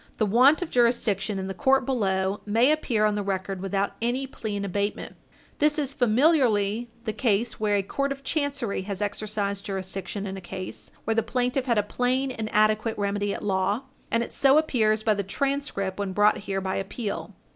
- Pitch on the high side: Yes, high, 215 Hz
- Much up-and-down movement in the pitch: No, average, 4.0 semitones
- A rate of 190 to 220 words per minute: Yes, average, 195 wpm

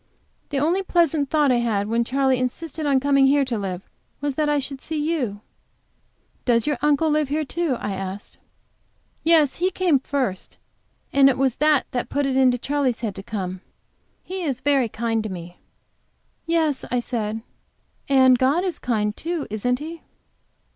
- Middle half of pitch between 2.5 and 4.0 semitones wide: No, average, 4.4 semitones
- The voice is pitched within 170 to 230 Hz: No, very high, 270 Hz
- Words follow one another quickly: No, average, 175 wpm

